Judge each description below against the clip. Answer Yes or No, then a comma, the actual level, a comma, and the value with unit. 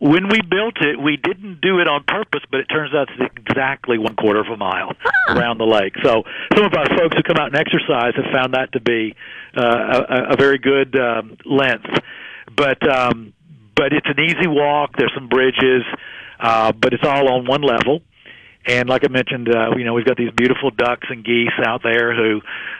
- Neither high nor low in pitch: No, low, 130 Hz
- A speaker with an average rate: No, fast, 225 wpm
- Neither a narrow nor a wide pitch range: Yes, average, 3.6 semitones